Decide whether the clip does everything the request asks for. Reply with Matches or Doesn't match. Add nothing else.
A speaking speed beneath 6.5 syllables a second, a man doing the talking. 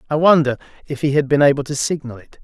Doesn't match